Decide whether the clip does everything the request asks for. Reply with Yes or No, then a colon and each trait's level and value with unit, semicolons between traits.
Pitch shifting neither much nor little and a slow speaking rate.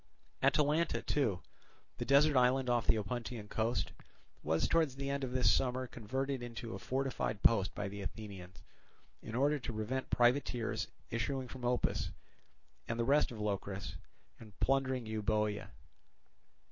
No: average, 3.7 semitones; average, 145 wpm